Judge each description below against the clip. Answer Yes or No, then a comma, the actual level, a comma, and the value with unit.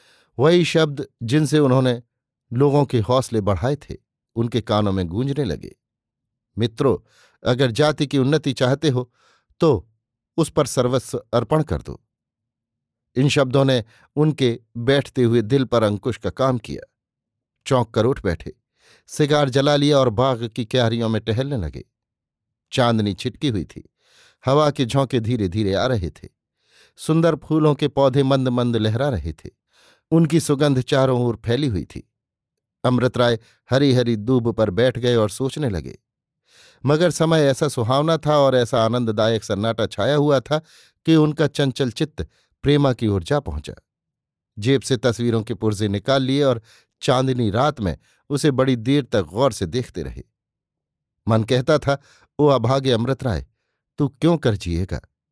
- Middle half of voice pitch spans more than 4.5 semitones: No, average, 3.8 semitones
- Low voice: Yes, low, 130 Hz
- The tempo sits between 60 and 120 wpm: No, average, 155 wpm